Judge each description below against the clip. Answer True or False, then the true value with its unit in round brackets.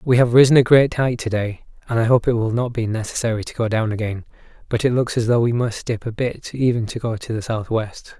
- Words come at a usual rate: False (265 wpm)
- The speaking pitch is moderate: False (115 Hz)